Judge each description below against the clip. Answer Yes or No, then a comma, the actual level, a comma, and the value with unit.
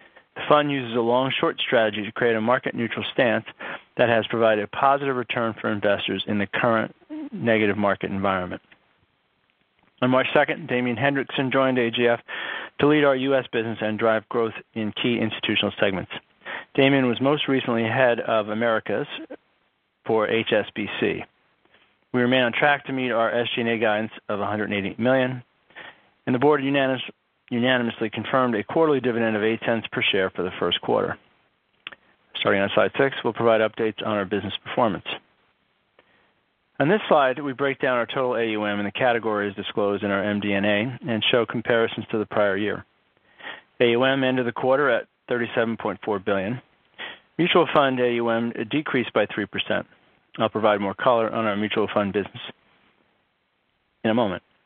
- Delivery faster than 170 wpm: No, average, 160 wpm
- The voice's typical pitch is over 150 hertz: No, low, 115 Hz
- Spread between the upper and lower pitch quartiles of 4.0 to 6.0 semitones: No, average, 3.4 semitones